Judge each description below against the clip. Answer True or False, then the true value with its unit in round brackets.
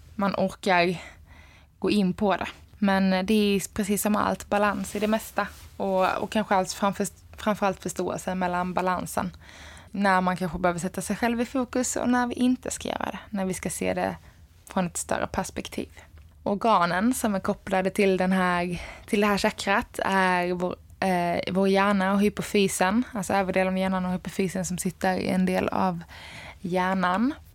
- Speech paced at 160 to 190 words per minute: True (180 wpm)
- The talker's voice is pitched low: False (190 Hz)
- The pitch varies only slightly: True (2.2 semitones)